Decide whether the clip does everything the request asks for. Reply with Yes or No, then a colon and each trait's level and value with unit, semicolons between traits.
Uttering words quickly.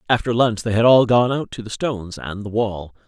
Yes: fast, 255 wpm